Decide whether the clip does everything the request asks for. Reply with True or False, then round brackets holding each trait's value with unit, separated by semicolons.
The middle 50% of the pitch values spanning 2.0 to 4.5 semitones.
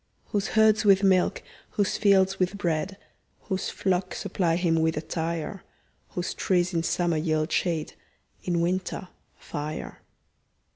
True (2.8 semitones)